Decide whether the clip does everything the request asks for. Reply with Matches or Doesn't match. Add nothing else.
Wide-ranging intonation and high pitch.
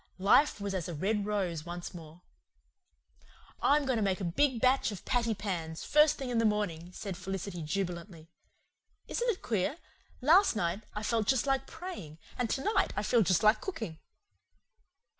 Matches